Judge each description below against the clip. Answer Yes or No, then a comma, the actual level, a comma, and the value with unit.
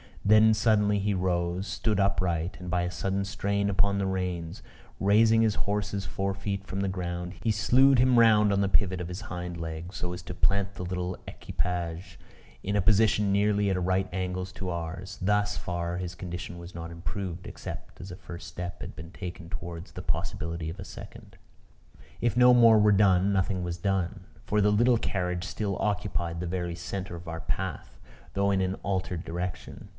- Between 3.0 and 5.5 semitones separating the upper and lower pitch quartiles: No, narrow, 2.5 semitones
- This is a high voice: No, very low, 95 Hz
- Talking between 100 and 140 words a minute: No, average, 190 wpm